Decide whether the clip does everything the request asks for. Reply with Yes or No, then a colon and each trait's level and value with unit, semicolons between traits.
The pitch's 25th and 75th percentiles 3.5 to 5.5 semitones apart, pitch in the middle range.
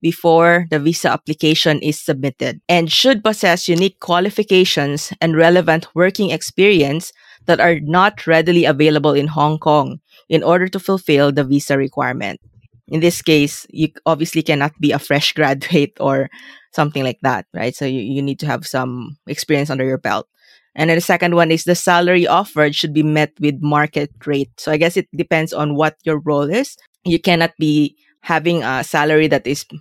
No: average, 3.0 semitones; medium, 155 Hz